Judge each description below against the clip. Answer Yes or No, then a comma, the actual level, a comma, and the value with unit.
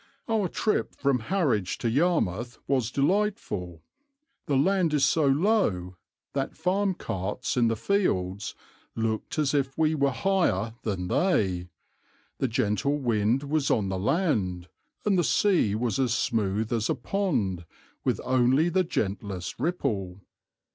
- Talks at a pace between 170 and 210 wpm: No, average, 140 wpm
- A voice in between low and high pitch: No, low, 130 Hz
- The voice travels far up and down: Yes, wide, 7.9 semitones